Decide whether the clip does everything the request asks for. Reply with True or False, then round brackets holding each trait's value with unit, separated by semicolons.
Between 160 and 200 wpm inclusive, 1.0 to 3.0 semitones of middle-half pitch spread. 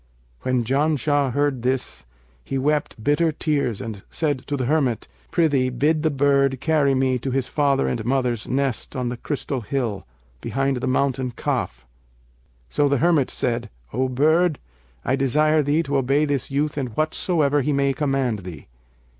True (165 wpm; 2.6 semitones)